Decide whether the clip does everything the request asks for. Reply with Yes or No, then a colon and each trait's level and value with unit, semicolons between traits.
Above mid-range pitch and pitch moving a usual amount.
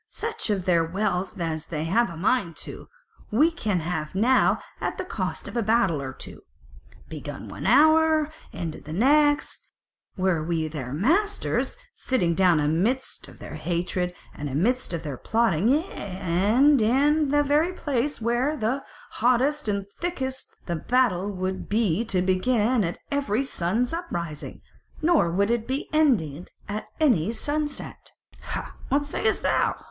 No: high, 215 Hz; wide, 7.9 semitones